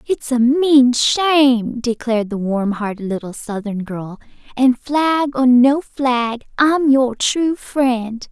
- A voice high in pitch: Yes, very high, 250 Hz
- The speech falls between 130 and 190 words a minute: Yes, average, 145 wpm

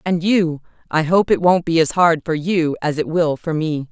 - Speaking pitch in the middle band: Yes, medium, 165 Hz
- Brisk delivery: Yes, fast, 230 wpm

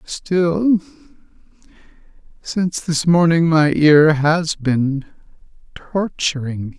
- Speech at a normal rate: No, slow, 90 wpm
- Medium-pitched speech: Yes, medium, 160 Hz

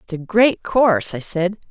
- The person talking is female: Yes, female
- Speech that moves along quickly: Yes, fast, 210 wpm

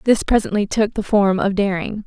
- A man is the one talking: No, female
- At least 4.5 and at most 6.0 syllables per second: Yes, 5.1 syllables/s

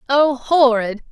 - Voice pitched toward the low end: No, very high, 260 Hz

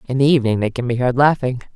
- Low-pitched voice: Yes, low, 130 Hz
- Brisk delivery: Yes, fast, 275 wpm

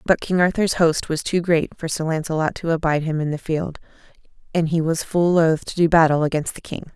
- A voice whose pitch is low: No, medium, 160 Hz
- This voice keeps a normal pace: No, fast, 235 wpm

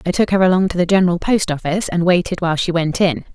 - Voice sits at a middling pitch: Yes, medium, 180 Hz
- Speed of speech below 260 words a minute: No, fast, 270 wpm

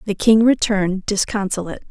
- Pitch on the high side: Yes, high, 200 Hz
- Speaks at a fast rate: No, slow, 125 wpm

